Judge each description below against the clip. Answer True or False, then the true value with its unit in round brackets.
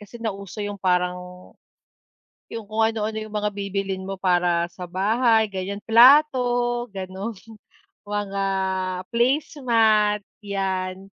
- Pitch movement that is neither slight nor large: True (3.0 semitones)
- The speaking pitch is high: True (205 Hz)